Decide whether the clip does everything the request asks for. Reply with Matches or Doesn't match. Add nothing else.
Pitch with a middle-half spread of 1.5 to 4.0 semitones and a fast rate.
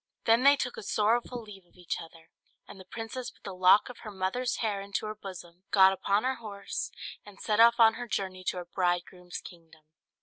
Matches